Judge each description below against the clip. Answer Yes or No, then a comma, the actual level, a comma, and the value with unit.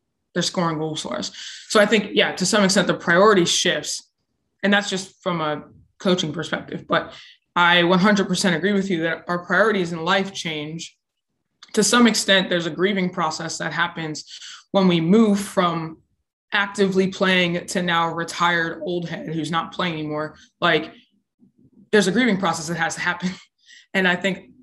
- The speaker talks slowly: No, average, 170 wpm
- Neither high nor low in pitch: Yes, medium, 180 Hz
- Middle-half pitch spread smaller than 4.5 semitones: Yes, average, 3.1 semitones